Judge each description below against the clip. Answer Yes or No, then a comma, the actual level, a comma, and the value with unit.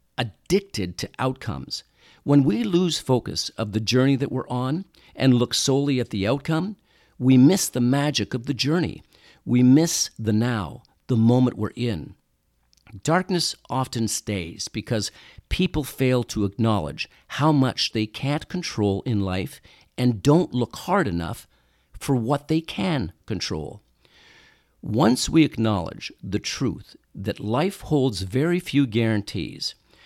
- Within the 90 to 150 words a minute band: Yes, average, 140 wpm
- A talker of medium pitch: No, low, 125 Hz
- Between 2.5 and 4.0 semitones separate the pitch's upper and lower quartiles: No, average, 5.2 semitones